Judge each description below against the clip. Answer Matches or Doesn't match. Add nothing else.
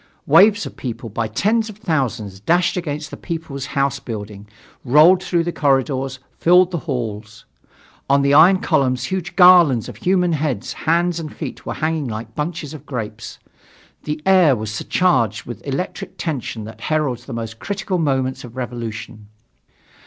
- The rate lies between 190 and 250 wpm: Doesn't match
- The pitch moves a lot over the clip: Matches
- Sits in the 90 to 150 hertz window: Matches